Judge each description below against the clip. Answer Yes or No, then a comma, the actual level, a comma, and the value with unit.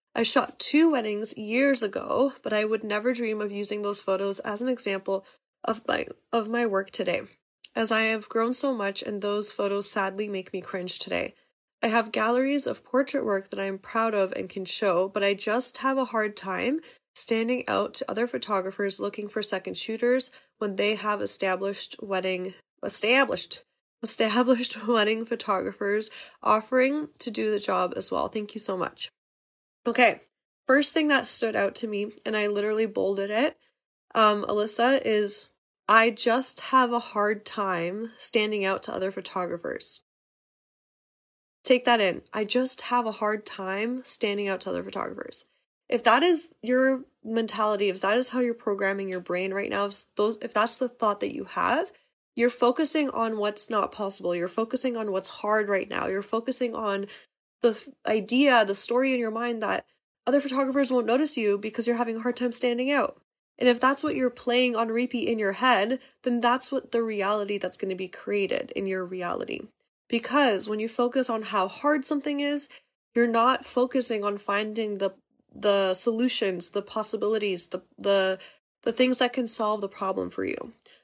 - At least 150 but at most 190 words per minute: Yes, average, 180 wpm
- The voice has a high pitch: Yes, high, 220 Hz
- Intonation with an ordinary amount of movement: Yes, average, 3.6 semitones